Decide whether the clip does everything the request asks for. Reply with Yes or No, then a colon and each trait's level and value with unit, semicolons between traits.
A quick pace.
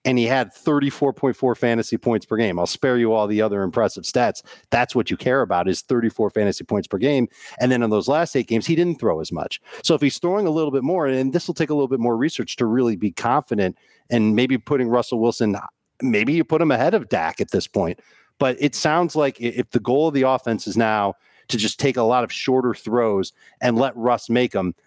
Yes: fast, 240 wpm